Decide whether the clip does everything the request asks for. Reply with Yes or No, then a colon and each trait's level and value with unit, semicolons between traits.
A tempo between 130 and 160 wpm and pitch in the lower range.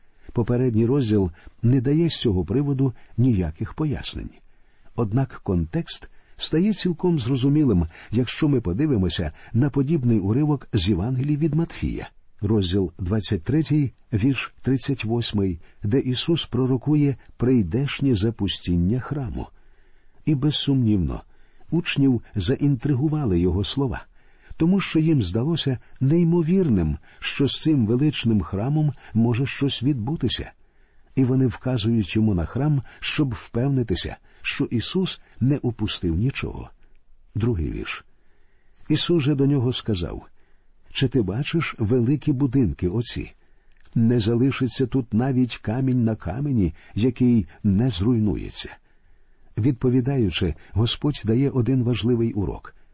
No: average, 110 wpm; low, 125 Hz